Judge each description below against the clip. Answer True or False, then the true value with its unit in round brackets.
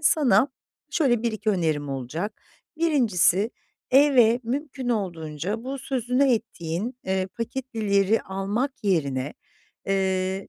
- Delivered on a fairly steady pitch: False (5.2 semitones)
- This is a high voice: True (215 Hz)